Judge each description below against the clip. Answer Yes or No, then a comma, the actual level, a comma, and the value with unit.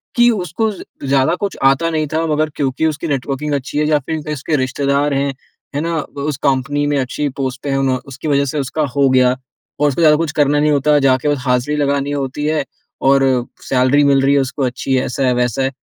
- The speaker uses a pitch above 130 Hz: Yes, medium, 140 Hz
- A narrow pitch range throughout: Yes, narrow, 2.1 semitones